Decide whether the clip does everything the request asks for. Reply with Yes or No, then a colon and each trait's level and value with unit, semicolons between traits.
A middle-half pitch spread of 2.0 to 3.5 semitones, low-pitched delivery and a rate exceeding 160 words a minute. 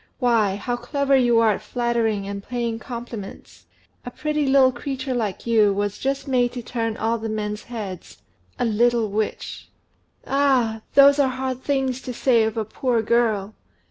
No: average, 3.0 semitones; high, 235 Hz; average, 170 wpm